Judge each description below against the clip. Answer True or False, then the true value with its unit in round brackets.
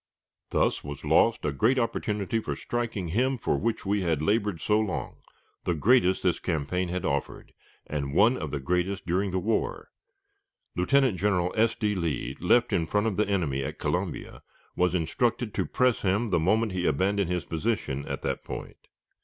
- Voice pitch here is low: True (95 Hz)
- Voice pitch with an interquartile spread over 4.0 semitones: True (4.6 semitones)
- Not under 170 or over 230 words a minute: True (180 wpm)